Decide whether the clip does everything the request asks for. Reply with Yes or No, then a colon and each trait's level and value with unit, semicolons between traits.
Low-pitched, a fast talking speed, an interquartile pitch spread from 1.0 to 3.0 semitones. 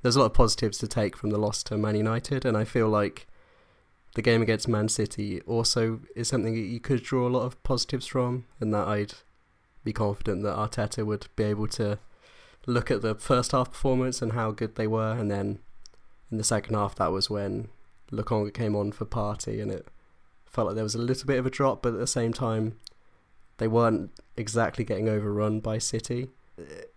Yes: low, 110 Hz; fast, 210 wpm; narrow, 2.6 semitones